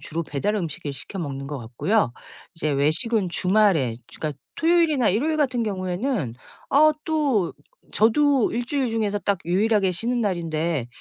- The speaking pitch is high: Yes, high, 200 Hz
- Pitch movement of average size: No, wide, 7.3 semitones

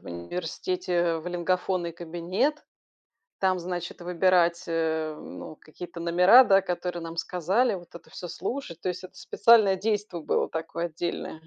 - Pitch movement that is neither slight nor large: No, narrow, 2.0 semitones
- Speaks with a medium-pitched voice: Yes, medium, 175 Hz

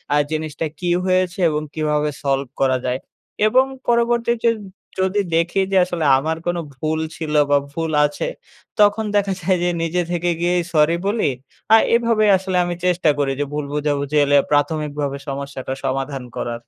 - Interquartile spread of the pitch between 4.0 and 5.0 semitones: Yes, average, 4.5 semitones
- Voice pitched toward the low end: No, medium, 160 Hz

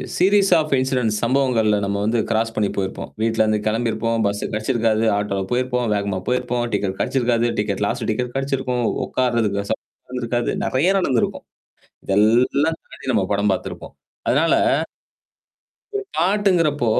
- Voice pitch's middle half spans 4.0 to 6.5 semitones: No, average, 3.4 semitones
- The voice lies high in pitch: No, low, 120 Hz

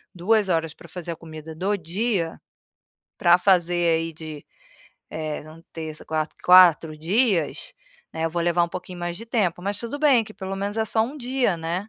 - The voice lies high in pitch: No, medium, 175 Hz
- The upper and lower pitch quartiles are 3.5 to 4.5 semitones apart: Yes, average, 4.0 semitones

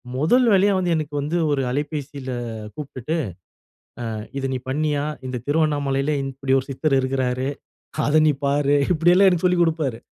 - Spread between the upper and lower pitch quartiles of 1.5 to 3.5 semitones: Yes, average, 3.0 semitones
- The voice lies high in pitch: No, medium, 145 Hz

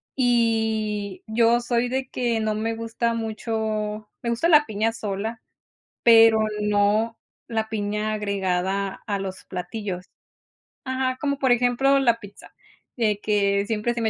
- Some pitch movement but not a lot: No, narrow, 2.3 semitones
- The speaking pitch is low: No, high, 220 Hz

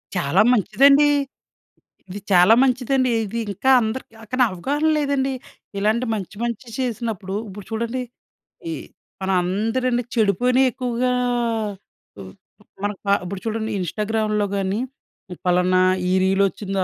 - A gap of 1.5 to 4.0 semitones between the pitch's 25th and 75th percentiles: No, average, 4.6 semitones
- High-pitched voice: Yes, high, 220 Hz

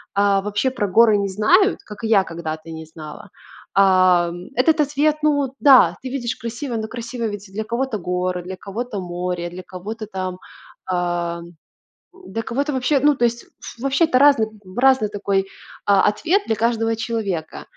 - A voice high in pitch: Yes, high, 215 Hz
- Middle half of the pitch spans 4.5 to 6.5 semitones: Yes, average, 5.3 semitones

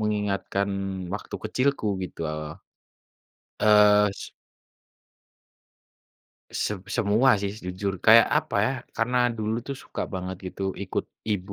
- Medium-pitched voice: No, low, 105 Hz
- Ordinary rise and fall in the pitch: No, narrow, 2.0 semitones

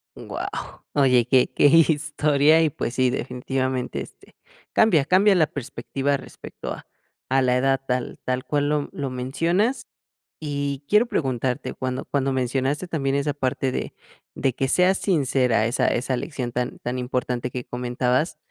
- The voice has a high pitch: No, low, 135 Hz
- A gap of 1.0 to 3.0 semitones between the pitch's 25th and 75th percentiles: Yes, average, 2.7 semitones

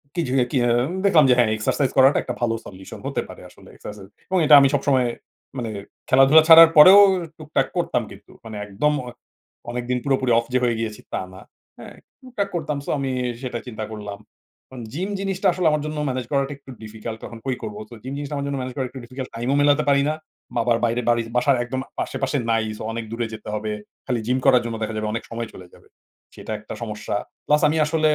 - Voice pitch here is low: Yes, low, 125 Hz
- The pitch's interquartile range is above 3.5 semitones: Yes, average, 4.1 semitones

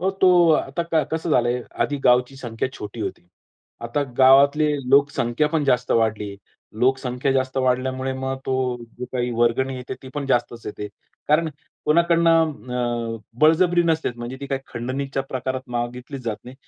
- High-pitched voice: No, low, 130 Hz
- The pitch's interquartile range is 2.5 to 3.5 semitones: Yes, average, 3.2 semitones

